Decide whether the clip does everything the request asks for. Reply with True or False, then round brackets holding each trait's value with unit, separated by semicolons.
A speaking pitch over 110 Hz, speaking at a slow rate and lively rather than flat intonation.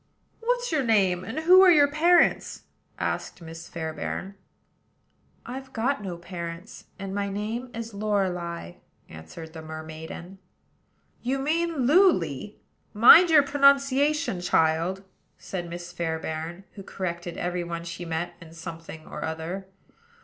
True (190 Hz; 130 wpm; 8.0 semitones)